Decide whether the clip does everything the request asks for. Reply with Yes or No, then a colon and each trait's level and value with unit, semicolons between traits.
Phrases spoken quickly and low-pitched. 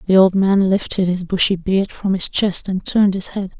No: fast, 235 wpm; high, 190 Hz